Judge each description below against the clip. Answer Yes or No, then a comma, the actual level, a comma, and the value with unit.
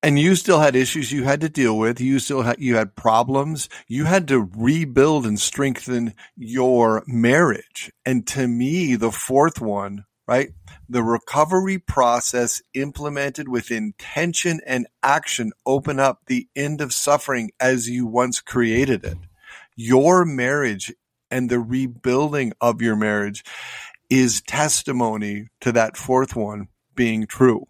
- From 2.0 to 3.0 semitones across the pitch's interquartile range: No, average, 3.5 semitones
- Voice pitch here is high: No, low, 125 Hz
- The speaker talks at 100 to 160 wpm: Yes, average, 145 wpm